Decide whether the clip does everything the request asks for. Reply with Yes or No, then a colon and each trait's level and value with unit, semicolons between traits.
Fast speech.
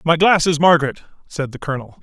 No: average, 180 wpm